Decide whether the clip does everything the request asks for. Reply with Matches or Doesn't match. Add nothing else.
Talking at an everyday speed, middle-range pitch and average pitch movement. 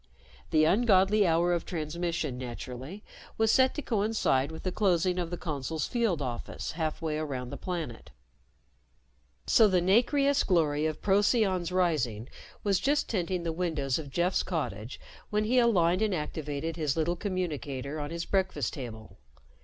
Matches